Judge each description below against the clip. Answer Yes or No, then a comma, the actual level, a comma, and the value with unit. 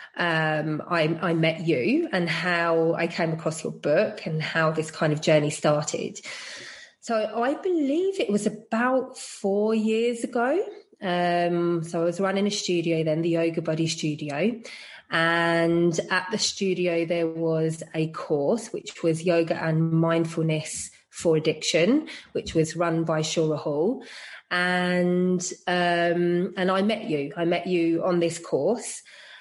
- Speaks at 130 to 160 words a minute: Yes, average, 150 wpm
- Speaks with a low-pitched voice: No, medium, 170 Hz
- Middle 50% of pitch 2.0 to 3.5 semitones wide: Yes, average, 3.1 semitones